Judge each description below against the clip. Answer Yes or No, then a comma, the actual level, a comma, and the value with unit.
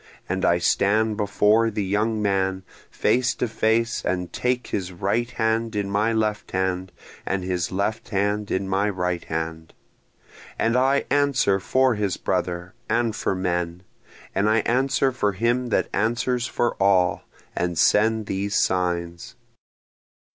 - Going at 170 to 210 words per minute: No, average, 145 wpm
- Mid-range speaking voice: No, low, 105 Hz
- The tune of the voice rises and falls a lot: No, average, 3.6 semitones